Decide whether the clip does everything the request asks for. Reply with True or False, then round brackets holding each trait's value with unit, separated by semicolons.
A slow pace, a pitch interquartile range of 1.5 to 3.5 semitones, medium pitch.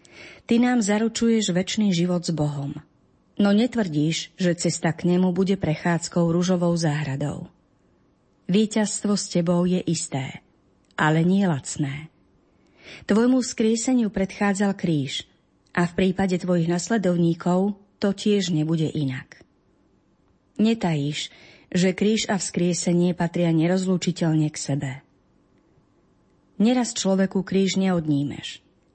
False (105 wpm; 4.0 semitones; 180 Hz)